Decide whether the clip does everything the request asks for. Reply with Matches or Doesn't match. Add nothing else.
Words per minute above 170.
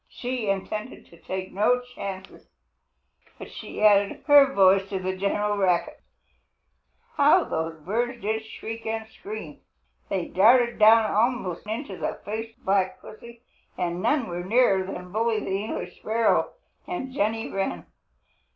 Doesn't match